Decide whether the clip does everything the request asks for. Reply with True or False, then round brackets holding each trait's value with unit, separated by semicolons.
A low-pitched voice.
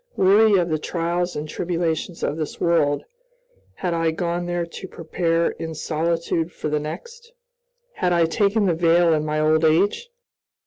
False (170 Hz)